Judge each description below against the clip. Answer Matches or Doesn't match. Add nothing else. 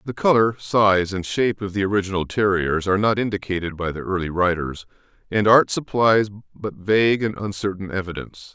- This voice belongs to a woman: Doesn't match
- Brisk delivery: Doesn't match